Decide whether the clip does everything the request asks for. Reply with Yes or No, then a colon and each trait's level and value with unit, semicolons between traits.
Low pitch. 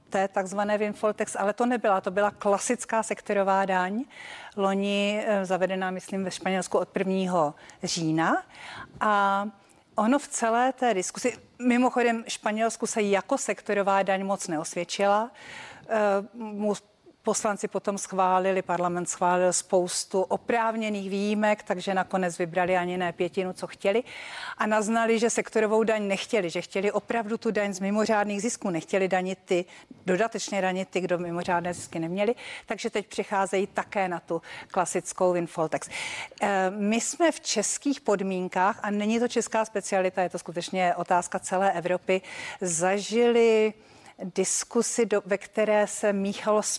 No: high, 200 Hz